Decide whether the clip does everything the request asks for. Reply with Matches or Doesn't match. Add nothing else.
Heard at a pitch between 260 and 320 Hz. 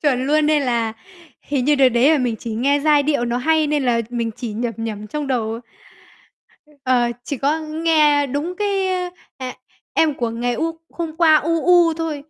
Matches